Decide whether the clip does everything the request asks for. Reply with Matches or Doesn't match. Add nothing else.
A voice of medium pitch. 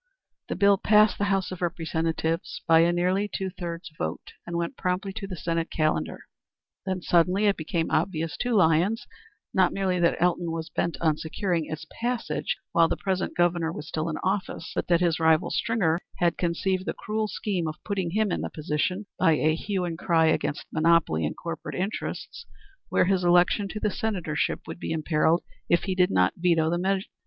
Matches